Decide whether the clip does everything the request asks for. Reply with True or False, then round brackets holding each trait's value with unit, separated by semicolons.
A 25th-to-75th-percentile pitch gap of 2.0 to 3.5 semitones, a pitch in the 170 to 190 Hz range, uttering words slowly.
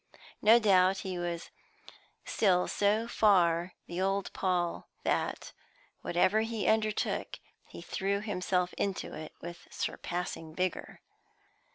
True (2.8 semitones; 185 Hz; 110 wpm)